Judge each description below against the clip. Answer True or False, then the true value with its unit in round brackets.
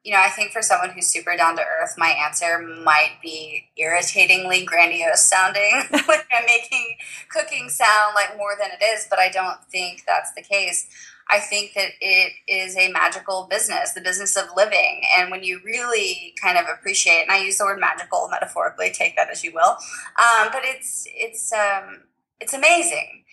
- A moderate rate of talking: True (190 wpm)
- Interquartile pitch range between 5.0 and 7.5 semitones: False (4.2 semitones)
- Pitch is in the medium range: False (195 Hz)